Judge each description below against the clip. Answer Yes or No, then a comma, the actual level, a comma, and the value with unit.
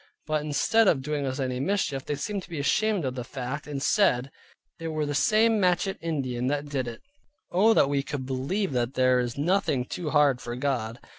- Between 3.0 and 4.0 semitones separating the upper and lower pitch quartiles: No, average, 4.9 semitones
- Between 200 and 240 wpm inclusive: Yes, fast, 205 wpm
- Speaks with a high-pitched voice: No, medium, 145 Hz